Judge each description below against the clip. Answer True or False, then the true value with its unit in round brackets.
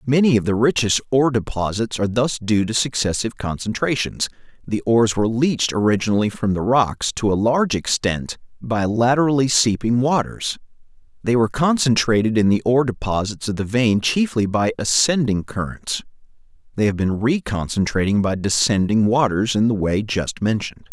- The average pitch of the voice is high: False (115 Hz)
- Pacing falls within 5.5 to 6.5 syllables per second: False (5.3 syllables/s)